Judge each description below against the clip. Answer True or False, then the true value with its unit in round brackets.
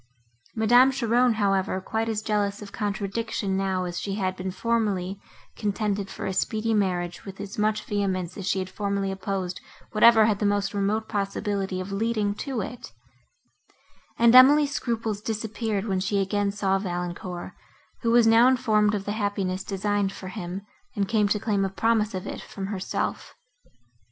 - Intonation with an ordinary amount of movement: False (2.3 semitones)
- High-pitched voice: True (205 Hz)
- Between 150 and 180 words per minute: True (165 wpm)